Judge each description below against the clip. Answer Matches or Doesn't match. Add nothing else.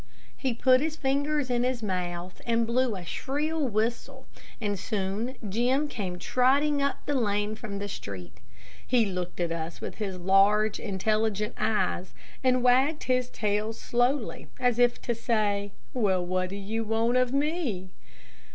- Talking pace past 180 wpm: Doesn't match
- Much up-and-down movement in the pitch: Doesn't match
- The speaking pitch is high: Matches